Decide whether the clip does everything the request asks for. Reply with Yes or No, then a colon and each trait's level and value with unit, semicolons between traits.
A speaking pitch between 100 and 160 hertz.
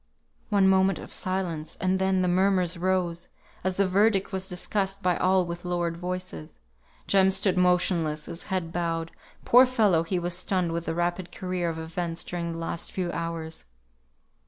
No: medium, 180 Hz